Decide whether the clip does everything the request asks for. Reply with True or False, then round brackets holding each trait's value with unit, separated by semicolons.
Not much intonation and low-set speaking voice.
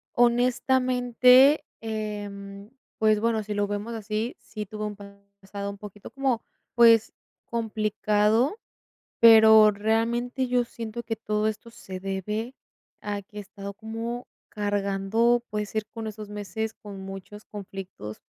False (2.2 semitones; 215 Hz)